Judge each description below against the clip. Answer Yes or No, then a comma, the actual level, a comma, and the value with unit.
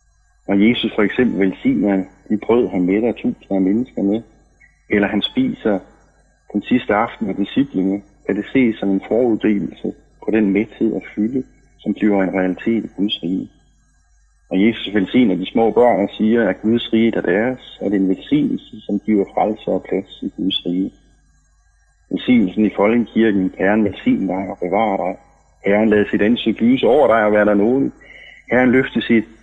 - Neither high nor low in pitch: No, low, 105 Hz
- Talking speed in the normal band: Yes, average, 175 wpm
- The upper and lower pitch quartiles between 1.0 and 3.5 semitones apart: Yes, average, 3.1 semitones